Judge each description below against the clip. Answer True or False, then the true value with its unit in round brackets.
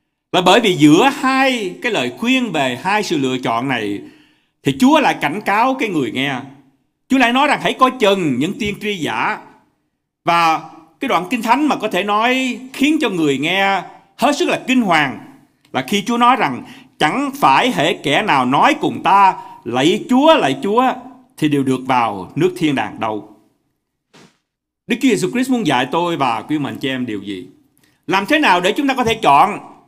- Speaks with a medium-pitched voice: False (215 Hz)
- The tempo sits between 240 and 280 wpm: False (195 wpm)